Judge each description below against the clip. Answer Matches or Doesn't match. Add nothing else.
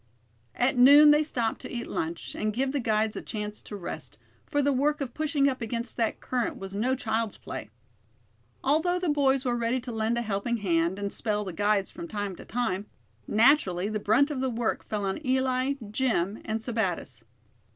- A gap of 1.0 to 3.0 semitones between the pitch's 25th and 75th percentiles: Doesn't match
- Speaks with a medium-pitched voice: Doesn't match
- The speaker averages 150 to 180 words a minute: Doesn't match